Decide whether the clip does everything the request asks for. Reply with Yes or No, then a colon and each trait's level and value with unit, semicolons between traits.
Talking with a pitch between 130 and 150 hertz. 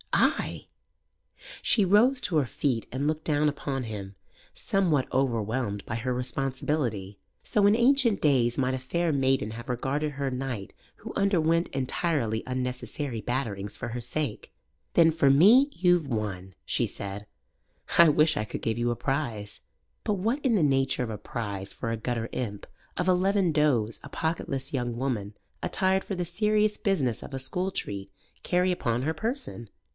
Yes: low, 135 Hz